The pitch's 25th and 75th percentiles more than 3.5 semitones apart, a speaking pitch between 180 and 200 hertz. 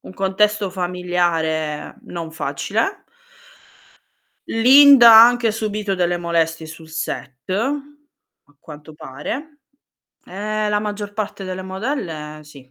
Yes: average, 5.3 semitones; high, 190 Hz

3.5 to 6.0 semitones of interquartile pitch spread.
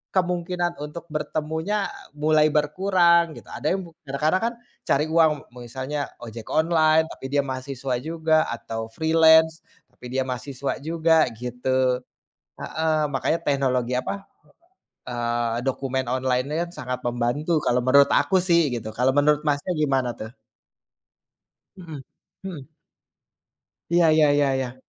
Yes: average, 4.0 semitones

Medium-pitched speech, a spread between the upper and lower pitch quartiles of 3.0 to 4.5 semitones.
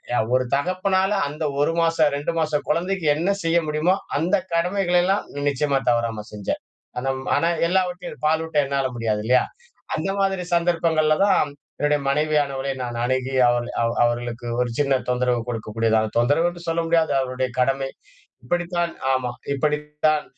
No: medium, 150 Hz; average, 5.0 semitones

